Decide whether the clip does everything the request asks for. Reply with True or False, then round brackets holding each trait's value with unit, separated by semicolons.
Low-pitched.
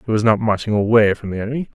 True (110 Hz)